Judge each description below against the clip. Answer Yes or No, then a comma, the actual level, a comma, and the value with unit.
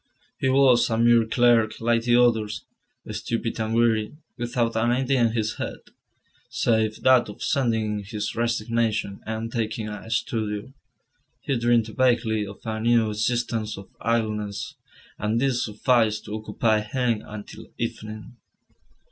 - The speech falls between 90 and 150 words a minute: Yes, average, 140 wpm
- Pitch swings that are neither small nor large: No, narrow, 1.8 semitones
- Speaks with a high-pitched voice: No, low, 115 Hz